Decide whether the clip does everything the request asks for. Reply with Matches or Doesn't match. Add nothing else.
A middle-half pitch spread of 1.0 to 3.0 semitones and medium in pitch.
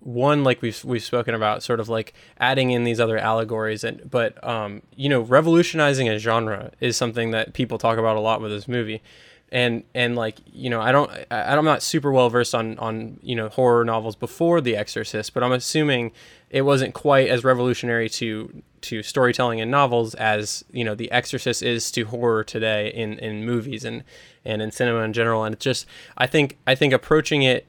Doesn't match